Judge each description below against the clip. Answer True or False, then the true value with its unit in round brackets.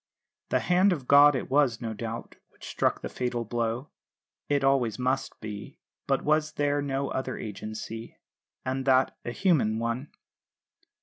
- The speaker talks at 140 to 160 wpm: True (150 wpm)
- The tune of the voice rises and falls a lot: False (3.6 semitones)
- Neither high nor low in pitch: False (130 Hz)